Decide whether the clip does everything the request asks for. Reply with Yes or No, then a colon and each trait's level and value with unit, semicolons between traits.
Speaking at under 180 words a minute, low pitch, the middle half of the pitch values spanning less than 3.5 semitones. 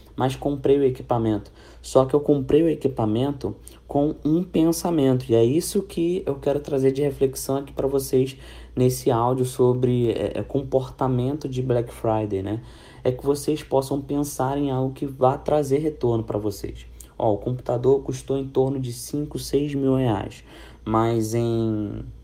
Yes: average, 160 wpm; low, 130 Hz; average, 2.9 semitones